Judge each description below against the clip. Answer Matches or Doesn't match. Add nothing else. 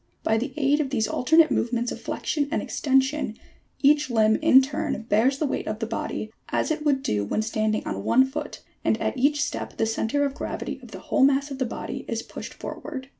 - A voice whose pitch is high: Matches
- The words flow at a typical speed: Doesn't match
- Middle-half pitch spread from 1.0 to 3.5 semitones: Doesn't match